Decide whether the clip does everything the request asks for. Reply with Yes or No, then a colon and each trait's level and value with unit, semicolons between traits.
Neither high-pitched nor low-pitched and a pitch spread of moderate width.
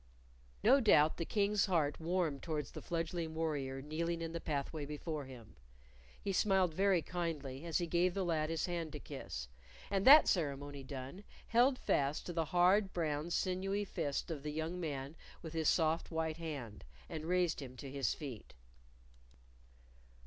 Yes: medium, 160 Hz; average, 3.6 semitones